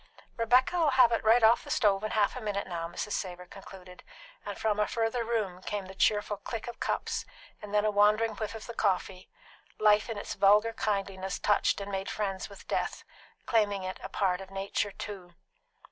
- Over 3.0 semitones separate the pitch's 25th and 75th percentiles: No, narrow, 2.4 semitones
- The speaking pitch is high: Yes, high, 205 Hz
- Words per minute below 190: No, average, 195 wpm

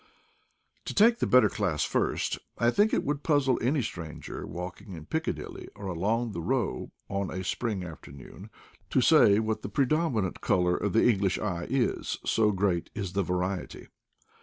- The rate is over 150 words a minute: Yes, average, 165 wpm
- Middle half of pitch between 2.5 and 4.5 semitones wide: No, average, 5.3 semitones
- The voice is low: Yes, low, 100 Hz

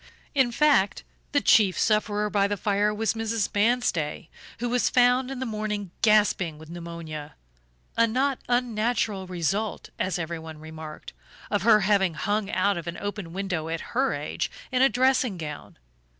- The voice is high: Yes, high, 205 Hz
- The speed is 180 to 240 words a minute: No, average, 160 wpm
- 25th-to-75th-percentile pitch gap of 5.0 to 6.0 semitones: Yes, average, 5.3 semitones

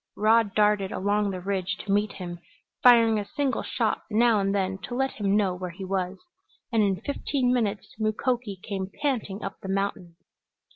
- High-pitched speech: Yes, high, 205 Hz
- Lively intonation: No, average, 2.8 semitones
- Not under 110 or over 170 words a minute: No, average, 180 wpm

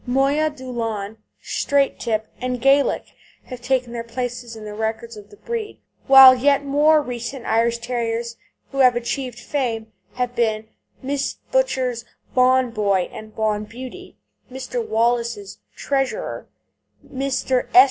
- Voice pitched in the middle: No, high, 245 Hz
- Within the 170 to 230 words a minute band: No, slow, 135 wpm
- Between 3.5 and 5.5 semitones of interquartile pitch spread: No, average, 2.9 semitones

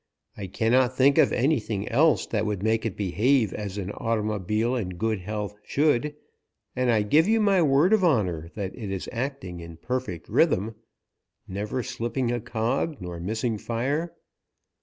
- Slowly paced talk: No, average, 160 wpm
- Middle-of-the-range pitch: No, low, 115 Hz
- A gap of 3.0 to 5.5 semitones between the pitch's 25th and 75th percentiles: Yes, average, 4.4 semitones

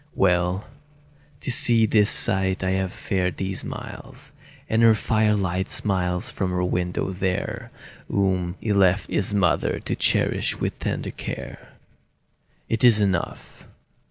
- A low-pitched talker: Yes, very low, 95 Hz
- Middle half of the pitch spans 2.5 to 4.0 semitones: Yes, average, 2.8 semitones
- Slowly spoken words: Yes, slow, 130 wpm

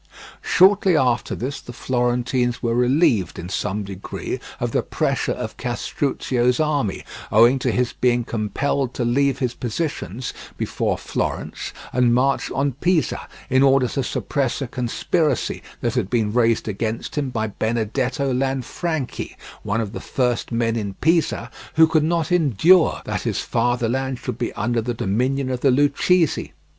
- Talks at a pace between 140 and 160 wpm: Yes, average, 150 wpm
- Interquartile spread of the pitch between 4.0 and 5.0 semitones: No, average, 3.1 semitones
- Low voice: Yes, low, 125 Hz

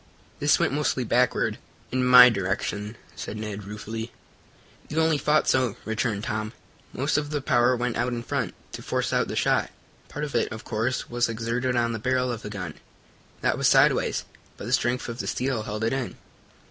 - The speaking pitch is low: Yes, low, 120 Hz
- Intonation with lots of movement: No, average, 2.8 semitones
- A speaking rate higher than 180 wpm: Yes, average, 195 wpm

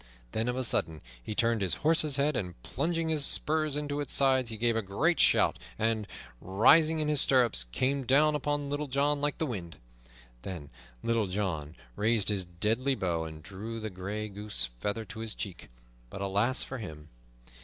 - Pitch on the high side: No, low, 115 Hz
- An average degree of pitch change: No, wide, 6.7 semitones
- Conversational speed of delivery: Yes, average, 185 wpm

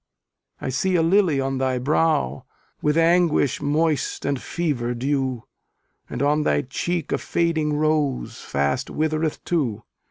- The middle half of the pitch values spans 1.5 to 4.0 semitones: Yes, average, 3.7 semitones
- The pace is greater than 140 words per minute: No, slow, 135 wpm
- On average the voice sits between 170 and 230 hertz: No, medium, 150 Hz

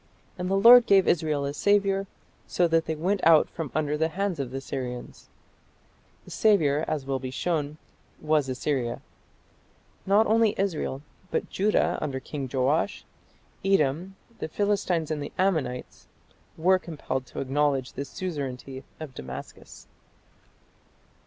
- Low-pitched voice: No, medium, 155 Hz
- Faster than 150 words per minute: No, average, 140 wpm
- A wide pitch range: Yes, wide, 5.7 semitones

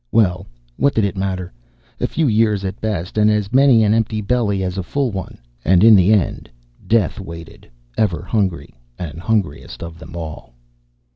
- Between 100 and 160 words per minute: No, average, 180 wpm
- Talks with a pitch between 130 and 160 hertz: No, low, 100 Hz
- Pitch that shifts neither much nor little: Yes, average, 3.6 semitones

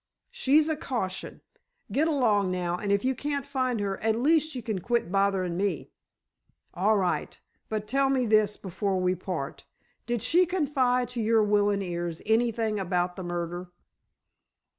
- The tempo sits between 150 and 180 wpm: Yes, average, 160 wpm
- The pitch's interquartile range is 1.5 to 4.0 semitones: No, wide, 5.5 semitones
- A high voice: Yes, high, 210 Hz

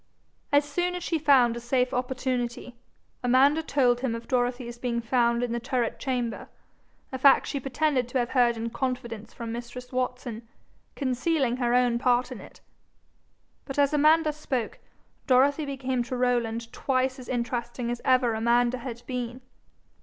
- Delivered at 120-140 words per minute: No, average, 160 wpm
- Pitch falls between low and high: No, very high, 250 Hz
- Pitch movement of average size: No, narrow, 1.8 semitones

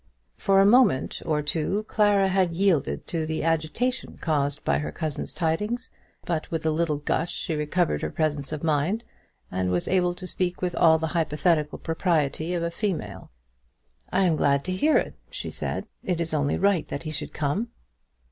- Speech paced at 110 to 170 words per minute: No, average, 185 wpm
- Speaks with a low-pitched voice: No, medium, 165 Hz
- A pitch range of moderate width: Yes, average, 3.5 semitones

